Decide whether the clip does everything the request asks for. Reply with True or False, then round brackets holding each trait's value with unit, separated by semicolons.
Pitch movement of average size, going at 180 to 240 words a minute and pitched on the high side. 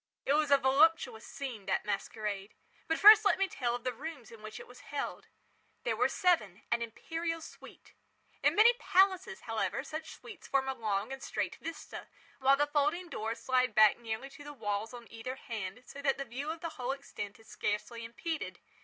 False (5.9 semitones; 195 wpm; 265 Hz)